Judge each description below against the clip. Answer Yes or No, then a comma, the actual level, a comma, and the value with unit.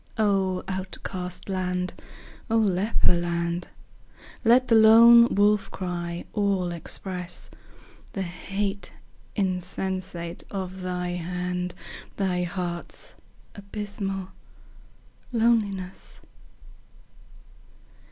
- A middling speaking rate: No, slow, 75 wpm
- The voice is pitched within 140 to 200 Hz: Yes, medium, 185 Hz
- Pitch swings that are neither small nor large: No, narrow, 2.2 semitones